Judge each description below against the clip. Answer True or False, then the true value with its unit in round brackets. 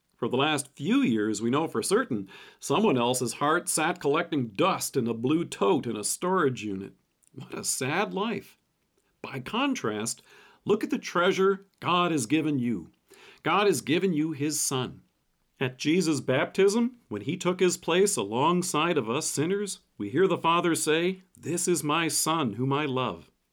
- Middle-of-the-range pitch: True (155 Hz)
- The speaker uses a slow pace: False (170 wpm)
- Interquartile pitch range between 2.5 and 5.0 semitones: False (5.6 semitones)